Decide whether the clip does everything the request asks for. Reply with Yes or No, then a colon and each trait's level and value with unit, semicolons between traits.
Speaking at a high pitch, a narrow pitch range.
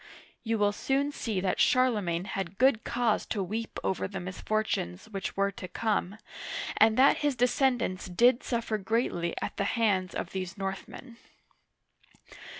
No: high, 215 Hz; average, 3.9 semitones